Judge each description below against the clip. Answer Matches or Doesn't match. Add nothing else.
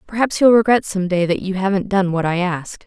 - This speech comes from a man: Doesn't match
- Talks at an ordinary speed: Doesn't match